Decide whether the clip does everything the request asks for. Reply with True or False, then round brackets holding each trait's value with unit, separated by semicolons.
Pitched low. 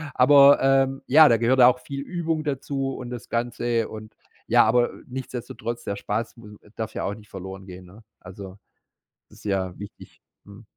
True (120 Hz)